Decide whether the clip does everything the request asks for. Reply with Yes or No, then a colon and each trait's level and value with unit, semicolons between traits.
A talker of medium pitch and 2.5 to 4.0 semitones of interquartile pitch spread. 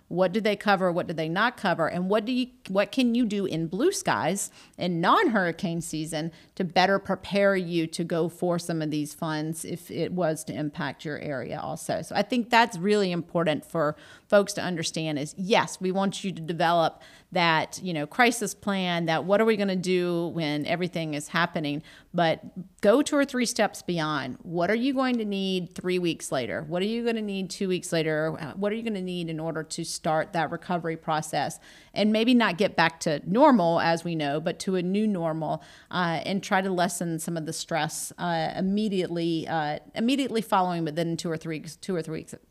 Yes: medium, 175 Hz; average, 3.7 semitones